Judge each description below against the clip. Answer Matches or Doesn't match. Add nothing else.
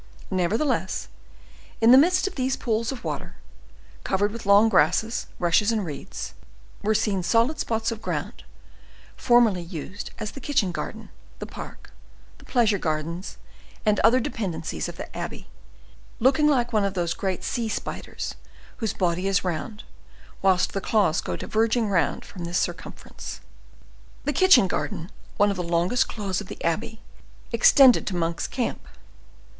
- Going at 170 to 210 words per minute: Doesn't match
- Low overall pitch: Doesn't match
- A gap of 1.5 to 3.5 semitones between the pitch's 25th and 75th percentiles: Doesn't match